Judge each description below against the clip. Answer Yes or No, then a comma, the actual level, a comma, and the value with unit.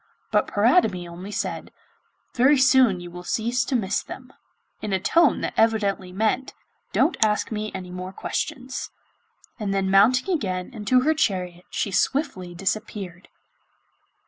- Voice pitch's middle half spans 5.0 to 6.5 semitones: Yes, wide, 5.4 semitones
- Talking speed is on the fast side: No, average, 145 wpm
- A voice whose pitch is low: No, high, 210 Hz